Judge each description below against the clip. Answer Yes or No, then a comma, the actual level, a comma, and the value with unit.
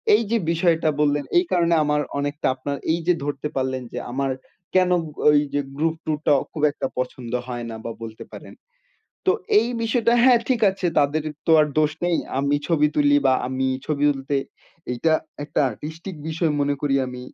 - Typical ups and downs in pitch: Yes, average, 3.4 semitones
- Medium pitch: Yes, medium, 150 Hz